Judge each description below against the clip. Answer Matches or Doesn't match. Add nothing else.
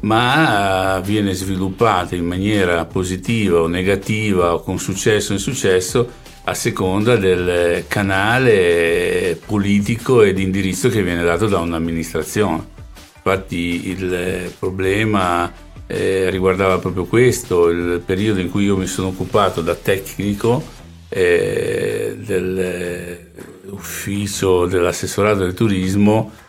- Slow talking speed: Matches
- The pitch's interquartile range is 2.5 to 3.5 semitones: Matches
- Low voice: Matches